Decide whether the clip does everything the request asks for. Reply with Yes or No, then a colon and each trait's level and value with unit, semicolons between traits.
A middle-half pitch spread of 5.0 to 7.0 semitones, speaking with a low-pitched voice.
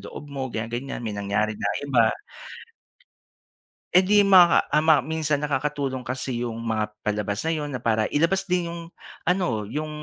Yes: wide, 5.6 semitones; low, 130 Hz